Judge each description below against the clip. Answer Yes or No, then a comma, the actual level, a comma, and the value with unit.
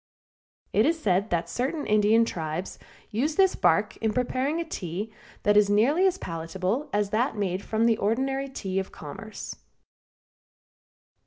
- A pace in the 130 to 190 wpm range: Yes, average, 150 wpm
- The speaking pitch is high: Yes, high, 220 Hz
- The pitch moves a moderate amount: No, wide, 5.7 semitones